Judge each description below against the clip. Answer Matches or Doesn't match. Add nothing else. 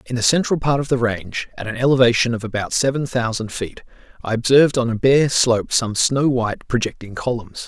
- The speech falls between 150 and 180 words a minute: Doesn't match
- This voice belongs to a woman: Doesn't match